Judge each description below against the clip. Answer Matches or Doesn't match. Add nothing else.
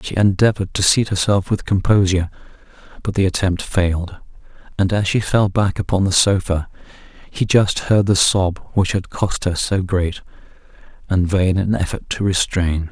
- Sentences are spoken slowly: Doesn't match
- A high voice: Doesn't match